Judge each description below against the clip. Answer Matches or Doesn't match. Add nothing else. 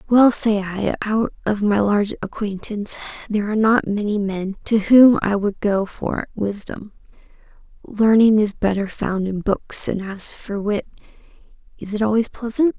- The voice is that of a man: Doesn't match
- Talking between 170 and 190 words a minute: Doesn't match